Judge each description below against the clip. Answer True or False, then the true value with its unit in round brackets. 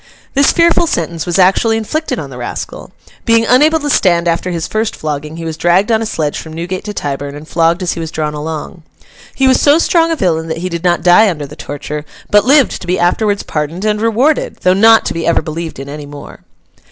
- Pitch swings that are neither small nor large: False (5.8 semitones)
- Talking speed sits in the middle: False (230 wpm)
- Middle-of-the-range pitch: True (175 Hz)